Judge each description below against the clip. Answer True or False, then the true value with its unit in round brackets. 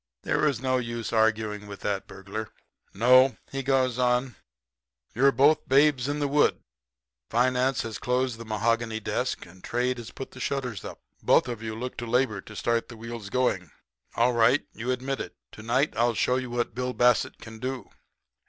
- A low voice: True (120 Hz)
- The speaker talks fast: False (185 wpm)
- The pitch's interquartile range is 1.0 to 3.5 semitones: True (2.4 semitones)